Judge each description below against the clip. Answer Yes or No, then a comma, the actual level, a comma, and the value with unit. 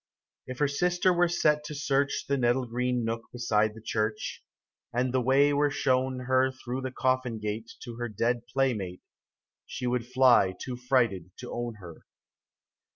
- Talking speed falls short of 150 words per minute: No, average, 165 wpm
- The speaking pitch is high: No, low, 125 Hz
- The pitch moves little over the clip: Yes, narrow, 2.3 semitones